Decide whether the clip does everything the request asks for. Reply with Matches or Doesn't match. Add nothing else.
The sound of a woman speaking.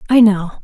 Matches